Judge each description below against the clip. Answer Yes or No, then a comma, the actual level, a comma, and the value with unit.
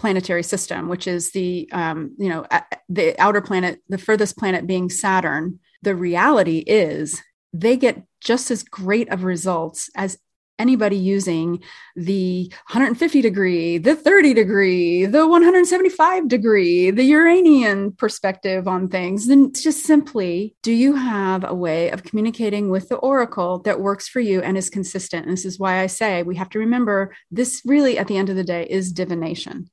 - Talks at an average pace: Yes, average, 170 wpm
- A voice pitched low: No, high, 195 Hz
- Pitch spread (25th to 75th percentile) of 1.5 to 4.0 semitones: No, average, 5.1 semitones